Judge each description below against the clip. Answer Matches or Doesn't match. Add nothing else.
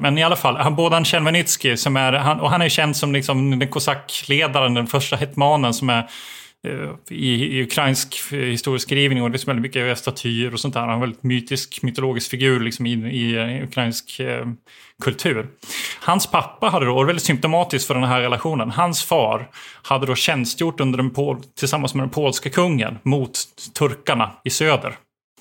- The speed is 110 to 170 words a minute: Doesn't match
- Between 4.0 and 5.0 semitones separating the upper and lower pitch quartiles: Doesn't match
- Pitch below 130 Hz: Doesn't match